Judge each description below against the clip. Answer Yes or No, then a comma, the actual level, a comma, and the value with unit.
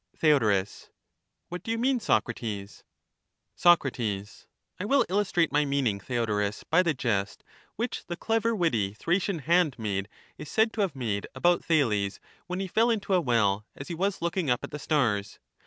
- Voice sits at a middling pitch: Yes, medium, 150 Hz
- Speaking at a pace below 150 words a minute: No, average, 165 wpm